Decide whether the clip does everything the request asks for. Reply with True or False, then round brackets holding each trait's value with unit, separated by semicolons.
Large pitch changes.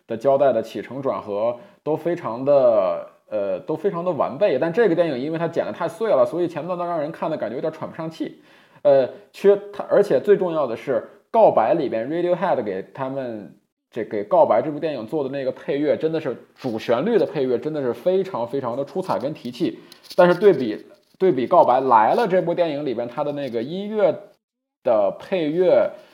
True (5.9 semitones)